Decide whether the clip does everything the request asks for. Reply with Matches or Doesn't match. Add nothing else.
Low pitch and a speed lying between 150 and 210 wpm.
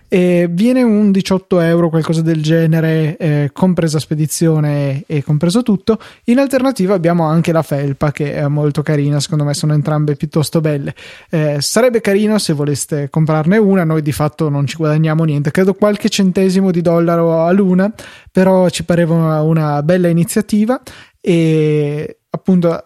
Doesn't match